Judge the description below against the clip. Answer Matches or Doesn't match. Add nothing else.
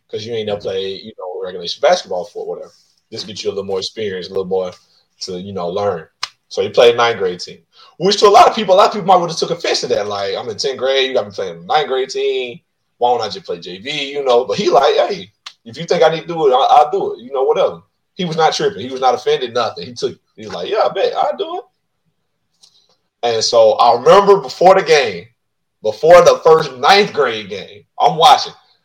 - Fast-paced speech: Matches